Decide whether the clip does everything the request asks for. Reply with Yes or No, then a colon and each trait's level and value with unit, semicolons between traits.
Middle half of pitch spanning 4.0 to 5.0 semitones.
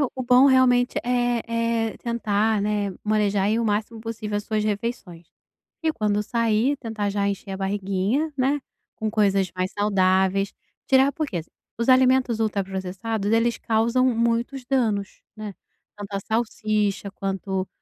No: average, 3.1 semitones